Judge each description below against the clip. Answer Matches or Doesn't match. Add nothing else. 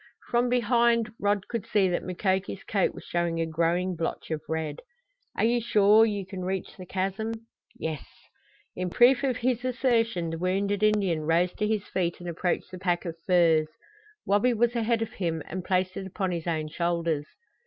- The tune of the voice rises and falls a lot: Doesn't match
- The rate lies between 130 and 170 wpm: Doesn't match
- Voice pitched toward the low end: Doesn't match